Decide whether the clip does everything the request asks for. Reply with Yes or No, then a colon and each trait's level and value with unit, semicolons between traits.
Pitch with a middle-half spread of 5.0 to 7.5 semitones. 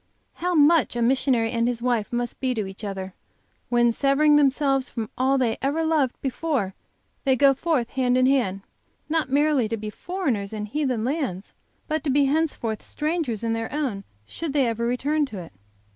No: average, 4.4 semitones